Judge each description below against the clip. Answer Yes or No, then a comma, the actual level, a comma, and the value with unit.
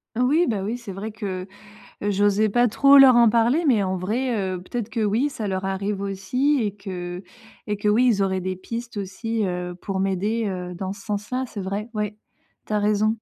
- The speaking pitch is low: No, high, 205 Hz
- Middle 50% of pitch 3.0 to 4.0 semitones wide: Yes, average, 3.3 semitones